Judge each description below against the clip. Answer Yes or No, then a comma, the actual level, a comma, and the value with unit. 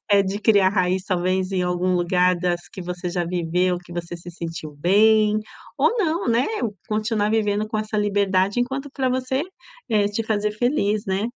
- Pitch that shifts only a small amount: No, average, 3.2 semitones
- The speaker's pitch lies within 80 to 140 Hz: No, high, 200 Hz